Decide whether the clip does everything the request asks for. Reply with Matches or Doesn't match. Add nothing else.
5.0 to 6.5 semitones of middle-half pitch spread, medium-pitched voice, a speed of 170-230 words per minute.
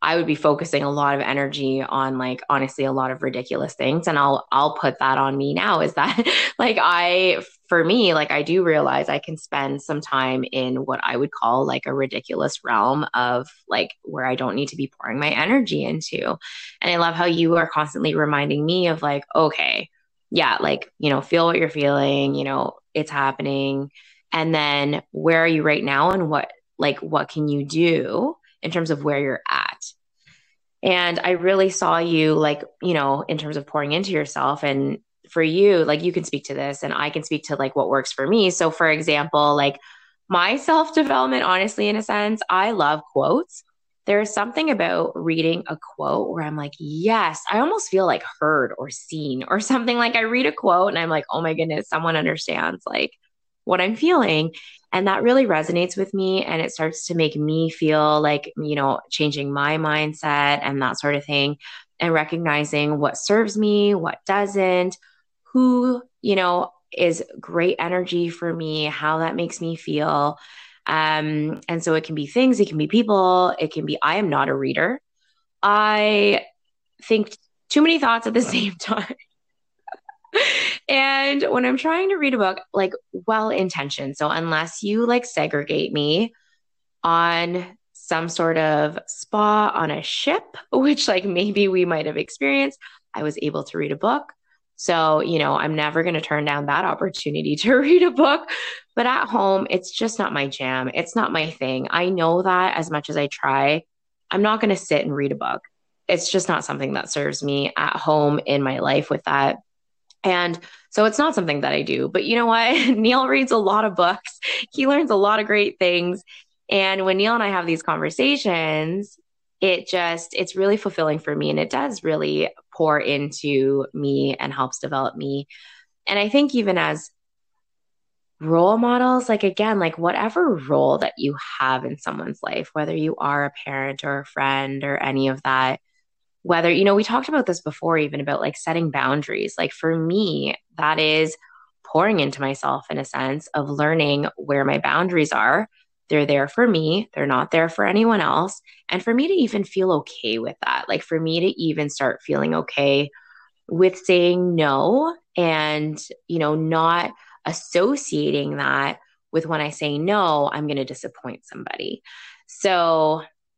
Matches